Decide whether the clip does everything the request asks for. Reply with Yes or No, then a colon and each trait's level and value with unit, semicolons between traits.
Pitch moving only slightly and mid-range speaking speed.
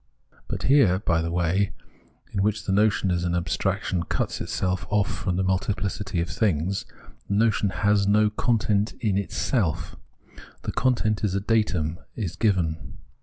No: average, 3.1 semitones; average, 155 wpm